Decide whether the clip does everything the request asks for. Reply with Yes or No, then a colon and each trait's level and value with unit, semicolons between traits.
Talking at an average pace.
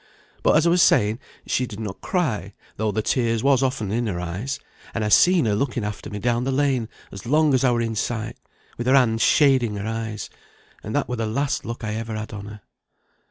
No: fast, 230 wpm